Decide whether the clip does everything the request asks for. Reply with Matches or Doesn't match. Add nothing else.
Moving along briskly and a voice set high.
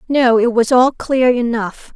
Doesn't match